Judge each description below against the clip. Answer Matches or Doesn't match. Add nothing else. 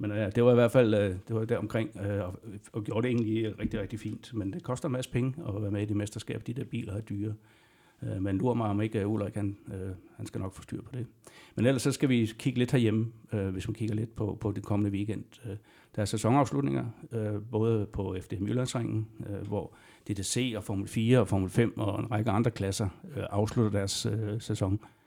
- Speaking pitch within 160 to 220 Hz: Doesn't match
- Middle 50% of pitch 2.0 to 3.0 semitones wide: Matches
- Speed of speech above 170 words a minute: Matches